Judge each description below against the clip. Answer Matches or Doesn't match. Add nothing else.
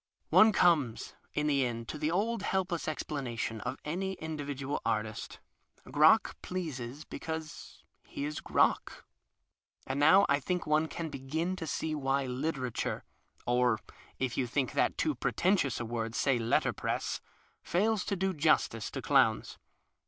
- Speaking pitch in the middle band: Matches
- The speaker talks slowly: Doesn't match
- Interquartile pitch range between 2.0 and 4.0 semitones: Doesn't match